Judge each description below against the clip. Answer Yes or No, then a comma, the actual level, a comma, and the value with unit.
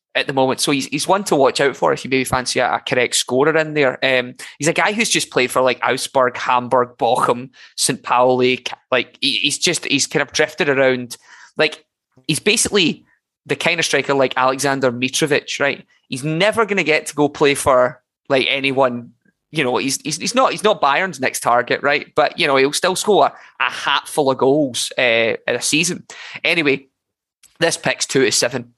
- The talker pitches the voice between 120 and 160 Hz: Yes, medium, 140 Hz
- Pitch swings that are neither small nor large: Yes, average, 3.8 semitones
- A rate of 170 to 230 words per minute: Yes, fast, 205 wpm